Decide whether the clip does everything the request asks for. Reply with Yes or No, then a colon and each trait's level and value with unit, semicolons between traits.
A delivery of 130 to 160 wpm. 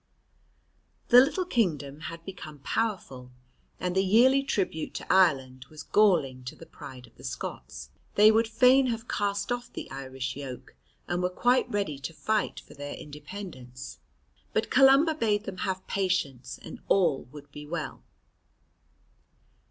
Yes: average, 150 wpm